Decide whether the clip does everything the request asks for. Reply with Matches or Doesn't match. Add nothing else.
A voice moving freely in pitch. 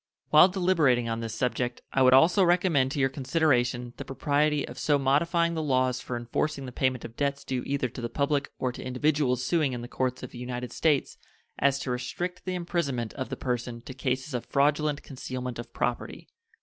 Doesn't match